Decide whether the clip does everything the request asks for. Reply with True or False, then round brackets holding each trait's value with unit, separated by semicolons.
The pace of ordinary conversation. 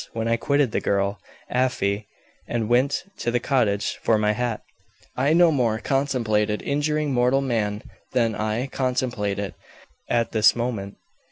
True (150 wpm)